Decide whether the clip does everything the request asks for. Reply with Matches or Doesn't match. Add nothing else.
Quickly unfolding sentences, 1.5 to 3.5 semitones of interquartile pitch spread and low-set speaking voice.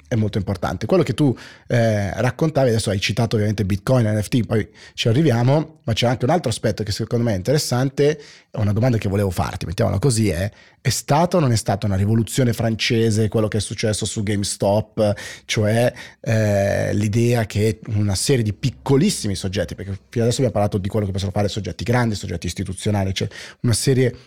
Matches